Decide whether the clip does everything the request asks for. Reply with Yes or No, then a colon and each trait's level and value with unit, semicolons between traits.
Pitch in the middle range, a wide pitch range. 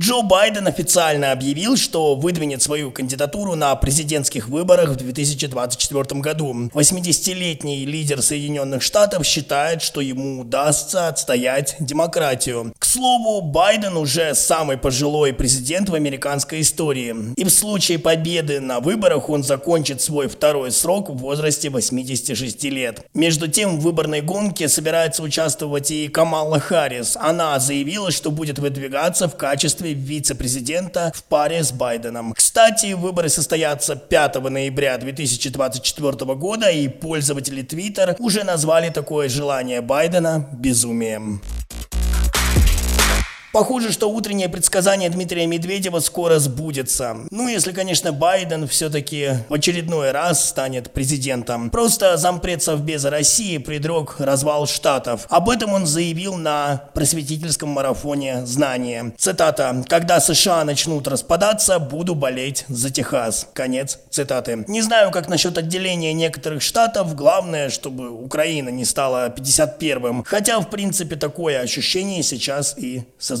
No: medium, 150 Hz; average, 4.1 semitones